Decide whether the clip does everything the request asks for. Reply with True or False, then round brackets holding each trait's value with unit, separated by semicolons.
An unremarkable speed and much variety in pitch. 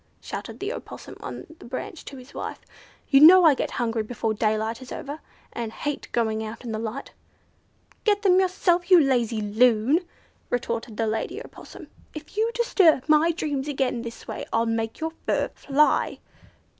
True (170 wpm; 6.0 semitones)